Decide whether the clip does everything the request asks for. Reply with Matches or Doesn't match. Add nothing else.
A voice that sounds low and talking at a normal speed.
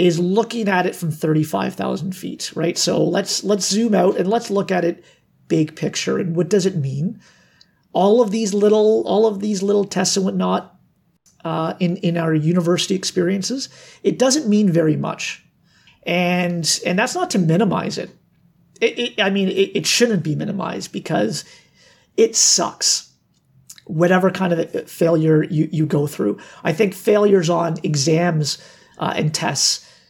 Doesn't match